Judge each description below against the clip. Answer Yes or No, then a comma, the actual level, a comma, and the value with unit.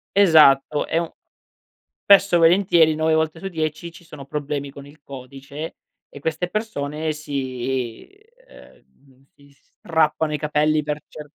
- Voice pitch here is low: No, medium, 150 Hz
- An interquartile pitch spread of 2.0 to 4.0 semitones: Yes, narrow, 2.4 semitones